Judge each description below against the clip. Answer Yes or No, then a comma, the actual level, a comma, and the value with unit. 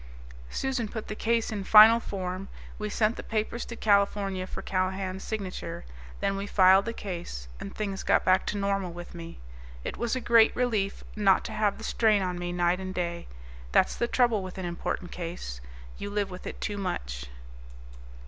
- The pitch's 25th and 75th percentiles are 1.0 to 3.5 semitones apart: Yes, average, 2.9 semitones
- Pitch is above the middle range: Yes, high, 195 Hz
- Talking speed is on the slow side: No, average, 185 wpm